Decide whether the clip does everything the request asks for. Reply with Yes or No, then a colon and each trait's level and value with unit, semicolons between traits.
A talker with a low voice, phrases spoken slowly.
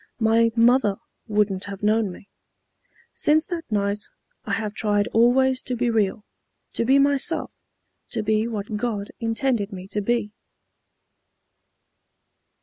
No: high, 225 Hz; slow, 130 wpm